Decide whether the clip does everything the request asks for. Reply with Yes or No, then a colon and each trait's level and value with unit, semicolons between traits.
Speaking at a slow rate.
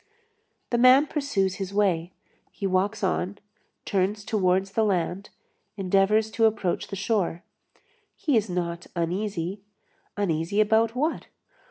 Yes: slow, 125 wpm